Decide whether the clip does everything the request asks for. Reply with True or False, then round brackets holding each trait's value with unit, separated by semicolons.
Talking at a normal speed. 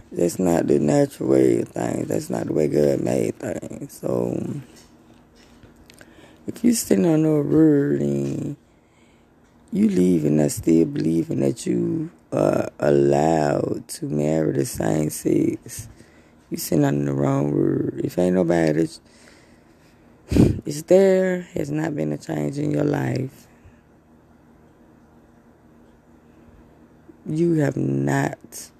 False (125 wpm)